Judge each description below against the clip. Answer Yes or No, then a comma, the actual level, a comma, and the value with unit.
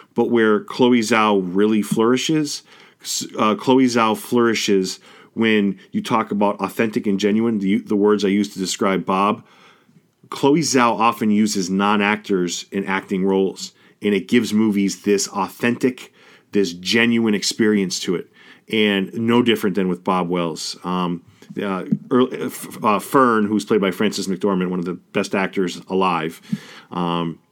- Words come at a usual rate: Yes, average, 145 wpm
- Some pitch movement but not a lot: Yes, average, 3.3 semitones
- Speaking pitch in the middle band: No, low, 105 Hz